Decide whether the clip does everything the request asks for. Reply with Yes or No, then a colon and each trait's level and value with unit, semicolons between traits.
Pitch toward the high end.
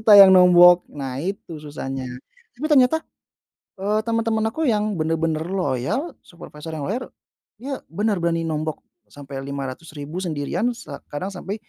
No: medium, 175 Hz